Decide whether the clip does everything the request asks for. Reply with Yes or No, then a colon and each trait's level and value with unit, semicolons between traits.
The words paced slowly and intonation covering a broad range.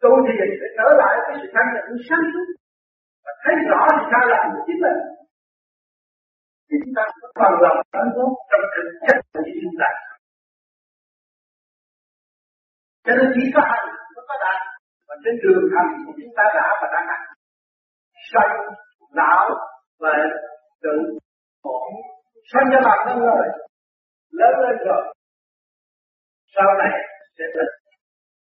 Yes: slow, 120 wpm; wide, 7.5 semitones